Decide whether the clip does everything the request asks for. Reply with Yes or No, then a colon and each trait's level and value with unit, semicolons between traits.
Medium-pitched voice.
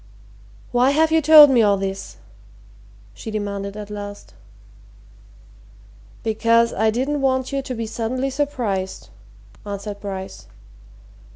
No: high, 225 Hz